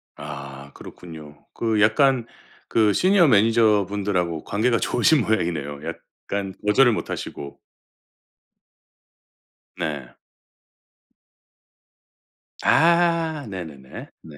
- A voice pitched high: No, low, 100 Hz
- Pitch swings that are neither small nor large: No, wide, 7.7 semitones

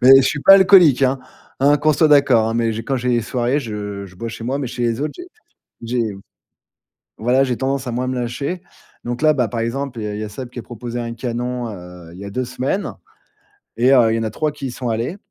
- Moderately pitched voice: No, low, 125 Hz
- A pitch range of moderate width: Yes, average, 3.0 semitones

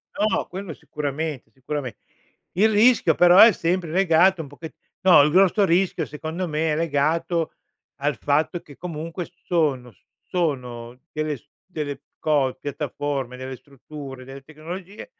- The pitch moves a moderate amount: Yes, average, 3.9 semitones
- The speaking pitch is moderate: Yes, medium, 155 Hz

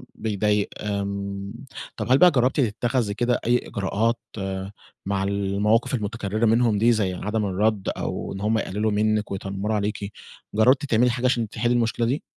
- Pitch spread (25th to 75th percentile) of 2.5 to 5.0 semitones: Yes, average, 2.8 semitones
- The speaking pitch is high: No, low, 105 Hz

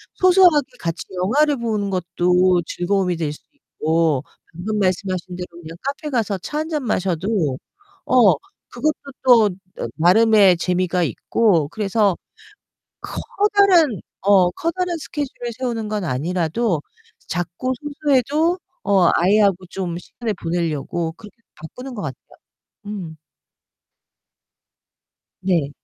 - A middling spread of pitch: No, wide, 6.3 semitones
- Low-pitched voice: No, high, 195 Hz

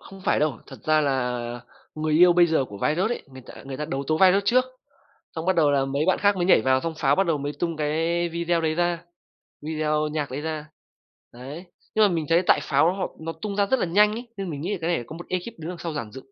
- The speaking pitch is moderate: Yes, medium, 160 Hz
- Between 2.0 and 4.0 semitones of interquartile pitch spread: Yes, average, 3.3 semitones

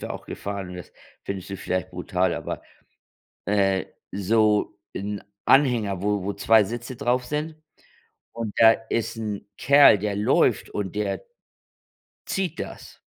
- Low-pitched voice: Yes, low, 105 Hz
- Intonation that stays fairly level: No, average, 3.0 semitones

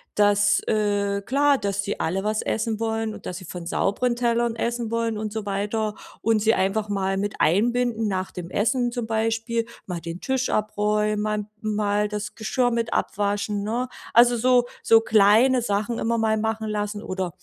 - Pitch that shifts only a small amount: Yes, narrow, 2.2 semitones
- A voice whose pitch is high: Yes, high, 215 Hz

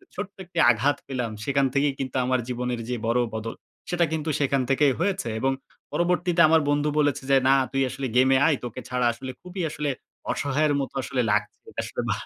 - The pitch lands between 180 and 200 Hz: No, low, 135 Hz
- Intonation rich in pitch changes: No, average, 3.4 semitones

